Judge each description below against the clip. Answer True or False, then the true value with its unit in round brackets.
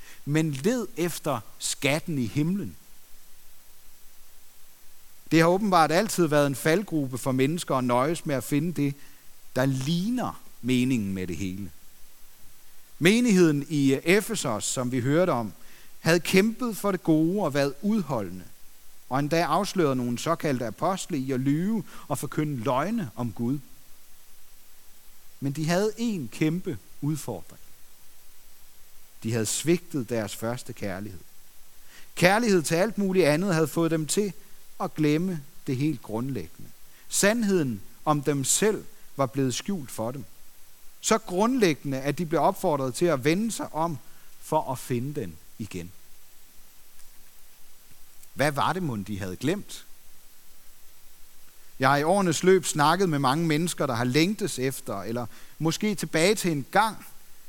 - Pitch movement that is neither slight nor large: False (5.9 semitones)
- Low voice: False (150 Hz)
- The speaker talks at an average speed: False (140 wpm)